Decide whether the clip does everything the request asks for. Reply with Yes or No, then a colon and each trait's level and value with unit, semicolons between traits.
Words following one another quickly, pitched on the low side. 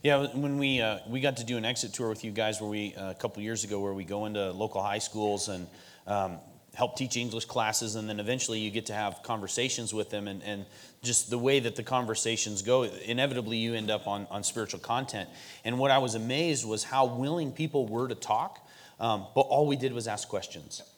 Yes: fast, 230 wpm; low, 115 Hz